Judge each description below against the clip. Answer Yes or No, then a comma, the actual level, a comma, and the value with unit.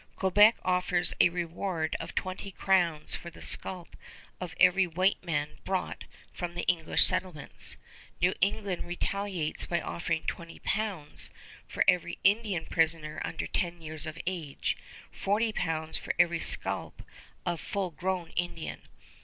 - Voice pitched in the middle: Yes, medium, 175 Hz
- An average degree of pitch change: No, narrow, 2.3 semitones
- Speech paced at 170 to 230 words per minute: No, slow, 135 wpm